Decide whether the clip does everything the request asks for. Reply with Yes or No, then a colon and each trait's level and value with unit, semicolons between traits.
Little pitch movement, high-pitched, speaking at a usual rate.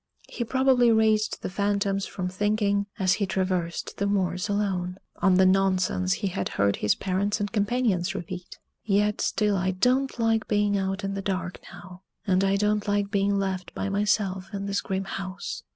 Yes: narrow, 1.9 semitones; high, 195 Hz; average, 180 wpm